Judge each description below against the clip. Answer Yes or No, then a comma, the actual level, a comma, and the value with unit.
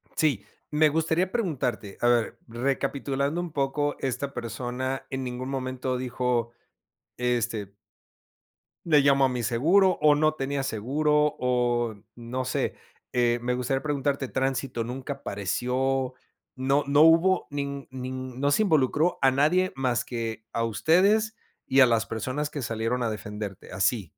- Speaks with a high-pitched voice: No, low, 130 Hz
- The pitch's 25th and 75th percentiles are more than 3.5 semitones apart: No, average, 3.2 semitones